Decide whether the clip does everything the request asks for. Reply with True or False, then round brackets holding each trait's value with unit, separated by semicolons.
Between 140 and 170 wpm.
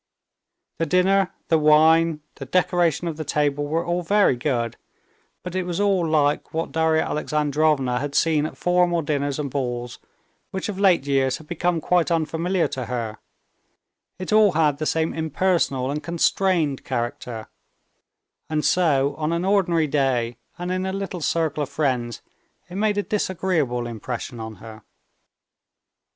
True (155 wpm)